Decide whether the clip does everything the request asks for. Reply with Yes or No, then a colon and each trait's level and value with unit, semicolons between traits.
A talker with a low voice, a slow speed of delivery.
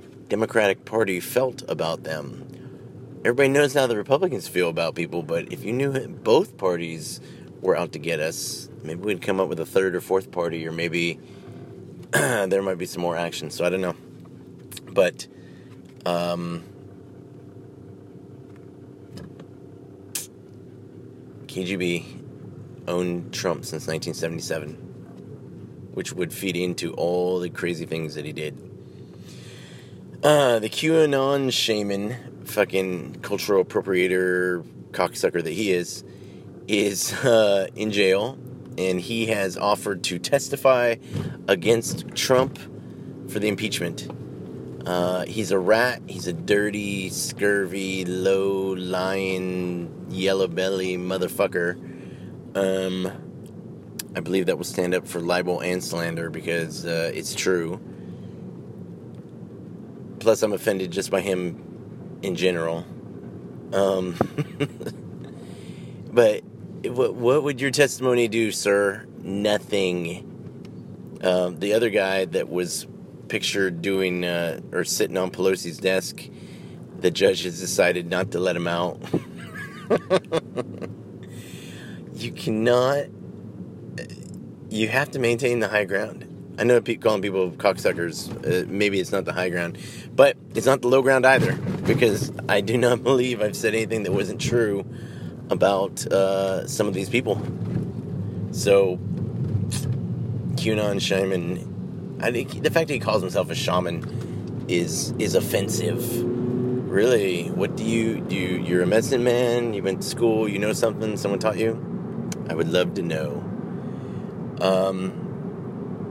Yes: very low, 95 Hz; slow, 130 wpm